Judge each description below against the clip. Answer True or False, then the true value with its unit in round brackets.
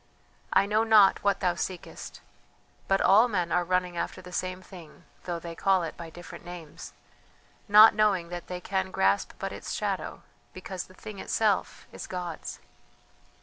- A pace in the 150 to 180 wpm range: True (165 wpm)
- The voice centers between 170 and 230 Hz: True (185 Hz)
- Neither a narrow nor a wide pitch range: False (2.1 semitones)